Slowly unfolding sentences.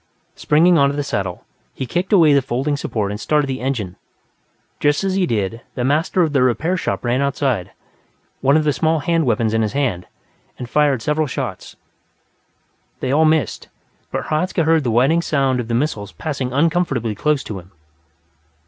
No: average, 180 wpm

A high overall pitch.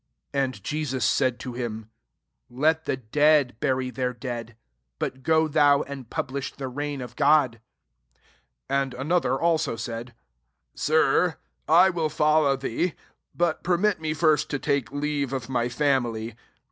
No: medium, 140 Hz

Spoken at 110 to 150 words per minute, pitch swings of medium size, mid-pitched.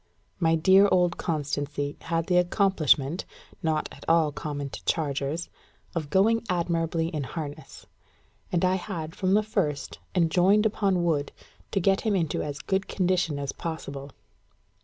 Yes: average, 145 wpm; average, 3.9 semitones; medium, 165 Hz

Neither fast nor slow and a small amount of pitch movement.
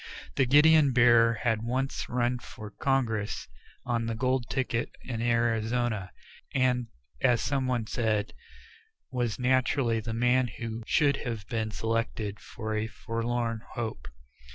No: slow, 130 wpm; narrow, 2.1 semitones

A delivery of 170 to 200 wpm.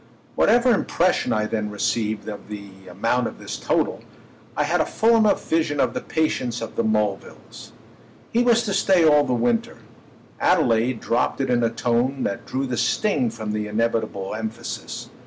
Yes: average, 175 wpm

